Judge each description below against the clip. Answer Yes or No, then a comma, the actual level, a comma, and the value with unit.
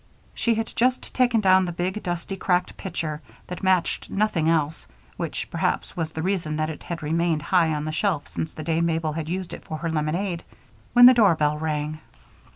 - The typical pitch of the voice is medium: Yes, medium, 170 Hz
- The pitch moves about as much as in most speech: Yes, average, 3.3 semitones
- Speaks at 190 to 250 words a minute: Yes, average, 195 wpm